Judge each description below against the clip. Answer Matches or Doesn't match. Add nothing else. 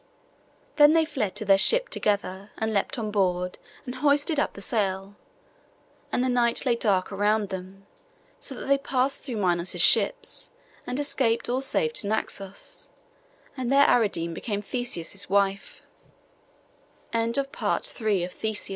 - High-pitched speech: Matches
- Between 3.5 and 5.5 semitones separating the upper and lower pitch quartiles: Matches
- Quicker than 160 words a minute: Doesn't match